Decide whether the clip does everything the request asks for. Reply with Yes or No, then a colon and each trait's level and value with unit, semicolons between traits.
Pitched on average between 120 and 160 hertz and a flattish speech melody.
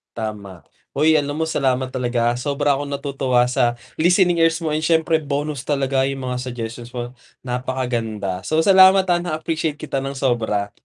No: low, 135 Hz; average, 4.3 semitones